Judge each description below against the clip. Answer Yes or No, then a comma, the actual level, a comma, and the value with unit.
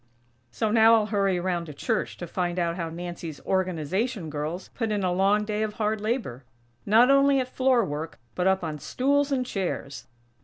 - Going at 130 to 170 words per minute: No, average, 190 wpm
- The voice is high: Yes, high, 195 Hz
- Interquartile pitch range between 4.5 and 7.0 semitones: Yes, average, 4.8 semitones